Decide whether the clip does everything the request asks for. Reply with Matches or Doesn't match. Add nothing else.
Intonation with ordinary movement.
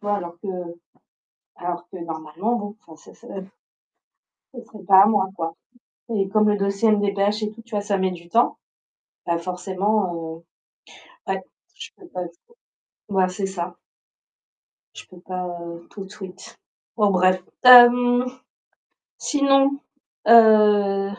Matches